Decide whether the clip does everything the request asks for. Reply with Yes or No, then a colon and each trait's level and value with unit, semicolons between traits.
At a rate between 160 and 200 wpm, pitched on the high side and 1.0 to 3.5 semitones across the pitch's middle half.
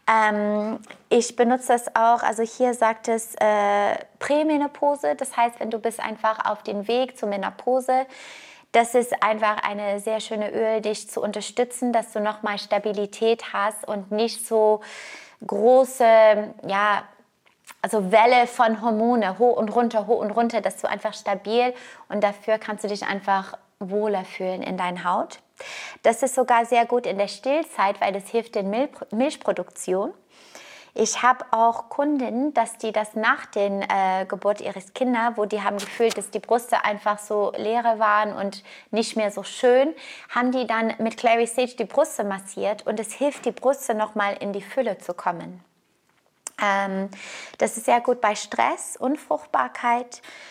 Yes: average, 165 wpm; high, 220 Hz; average, 2.8 semitones